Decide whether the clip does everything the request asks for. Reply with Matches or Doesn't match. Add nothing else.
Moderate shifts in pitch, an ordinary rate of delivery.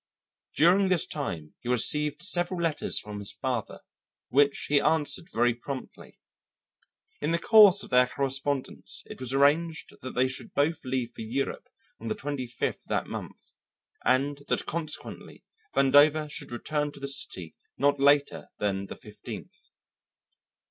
Matches